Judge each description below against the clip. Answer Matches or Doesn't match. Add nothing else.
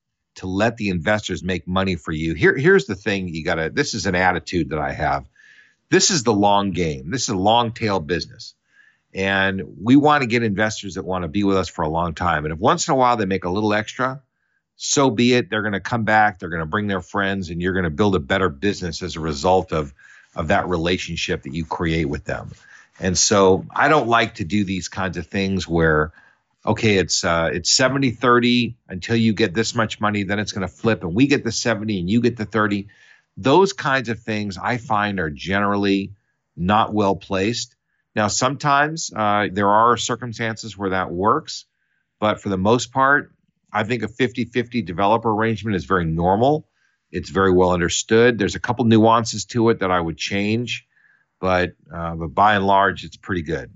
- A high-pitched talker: Doesn't match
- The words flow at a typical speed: Doesn't match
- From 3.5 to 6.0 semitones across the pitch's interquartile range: Matches